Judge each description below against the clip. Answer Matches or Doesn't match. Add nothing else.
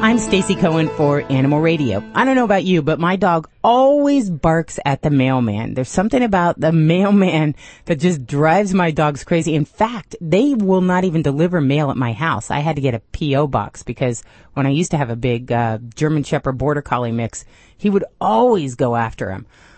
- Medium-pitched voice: Matches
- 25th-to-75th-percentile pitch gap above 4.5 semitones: Matches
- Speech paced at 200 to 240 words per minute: Matches